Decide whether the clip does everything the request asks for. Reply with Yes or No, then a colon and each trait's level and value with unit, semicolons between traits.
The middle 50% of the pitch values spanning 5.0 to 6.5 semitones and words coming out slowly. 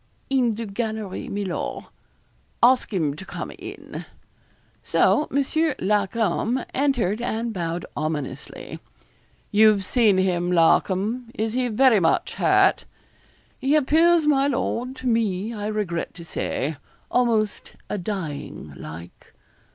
Yes: wide, 5.4 semitones; slow, 120 wpm